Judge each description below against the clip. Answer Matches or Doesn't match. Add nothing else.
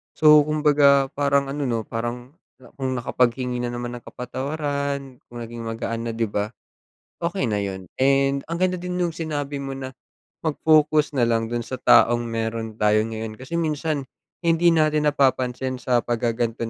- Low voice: Matches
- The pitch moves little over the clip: Doesn't match